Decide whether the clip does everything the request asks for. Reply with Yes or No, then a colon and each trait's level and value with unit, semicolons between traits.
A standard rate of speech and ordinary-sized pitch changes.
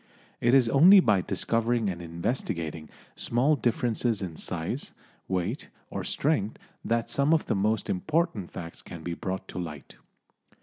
No: average, 145 wpm; wide, 5.9 semitones